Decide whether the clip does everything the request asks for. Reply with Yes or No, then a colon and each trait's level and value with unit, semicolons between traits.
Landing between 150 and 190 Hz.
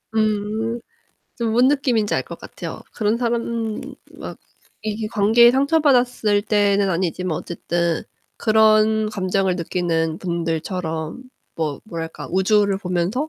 No: high, 210 Hz